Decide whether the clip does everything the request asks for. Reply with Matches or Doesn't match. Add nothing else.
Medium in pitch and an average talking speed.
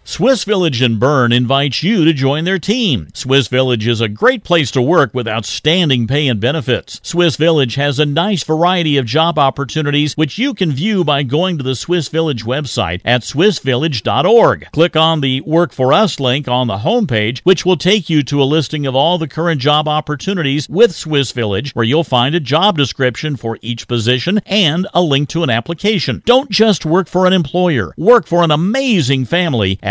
Matches